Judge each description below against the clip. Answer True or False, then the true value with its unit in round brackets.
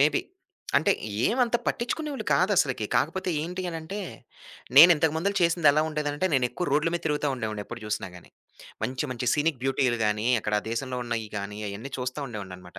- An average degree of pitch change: False (6.4 semitones)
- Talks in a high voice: False (140 Hz)